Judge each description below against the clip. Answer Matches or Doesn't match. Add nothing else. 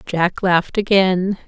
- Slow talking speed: Matches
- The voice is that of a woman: Matches